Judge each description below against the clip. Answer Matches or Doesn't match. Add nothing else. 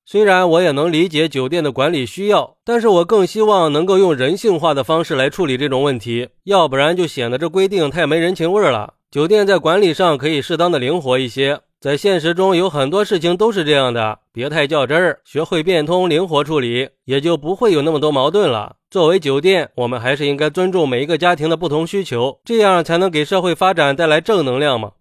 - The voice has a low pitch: Doesn't match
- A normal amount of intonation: Matches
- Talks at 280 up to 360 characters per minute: Matches